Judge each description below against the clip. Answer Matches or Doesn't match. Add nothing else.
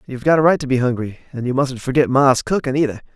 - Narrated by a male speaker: Matches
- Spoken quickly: Matches